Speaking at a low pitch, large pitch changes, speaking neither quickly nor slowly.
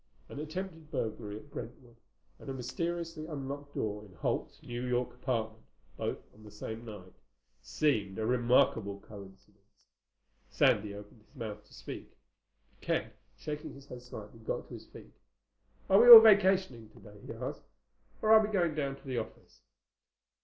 Yes: low, 125 Hz; wide, 6.4 semitones; average, 160 wpm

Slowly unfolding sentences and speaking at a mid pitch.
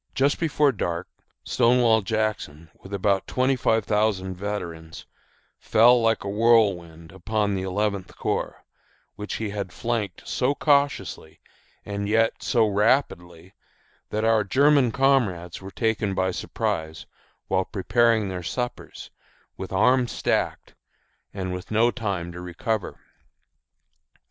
No: slow, 120 wpm; low, 105 Hz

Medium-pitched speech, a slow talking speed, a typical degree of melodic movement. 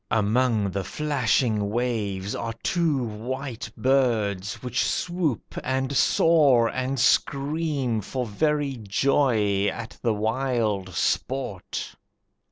No: low, 120 Hz; slow, 100 wpm; average, 4.4 semitones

